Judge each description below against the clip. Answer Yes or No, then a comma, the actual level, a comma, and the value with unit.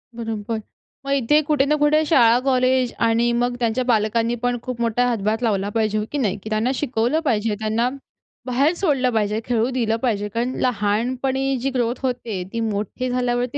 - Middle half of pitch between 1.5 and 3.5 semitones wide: Yes, narrow, 2.6 semitones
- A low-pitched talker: No, high, 240 Hz